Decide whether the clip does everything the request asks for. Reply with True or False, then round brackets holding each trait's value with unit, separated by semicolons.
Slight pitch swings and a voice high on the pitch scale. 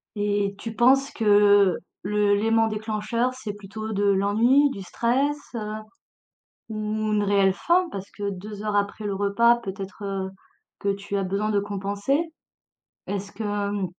True (2.0 semitones; 205 Hz)